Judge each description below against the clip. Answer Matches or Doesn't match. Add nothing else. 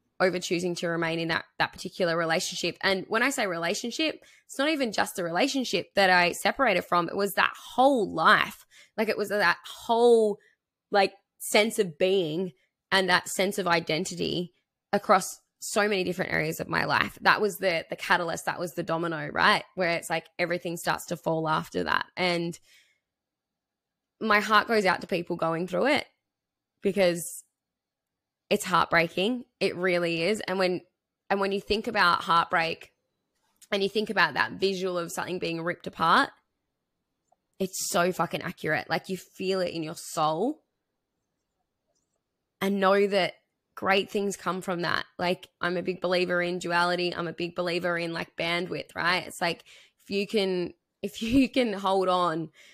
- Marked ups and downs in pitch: Doesn't match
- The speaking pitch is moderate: Matches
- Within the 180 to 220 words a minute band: Doesn't match